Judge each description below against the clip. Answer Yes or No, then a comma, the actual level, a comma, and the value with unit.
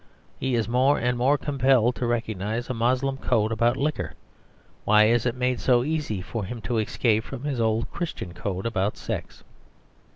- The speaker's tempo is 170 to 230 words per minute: Yes, average, 175 wpm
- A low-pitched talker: Yes, low, 120 Hz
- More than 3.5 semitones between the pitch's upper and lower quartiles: No, average, 2.8 semitones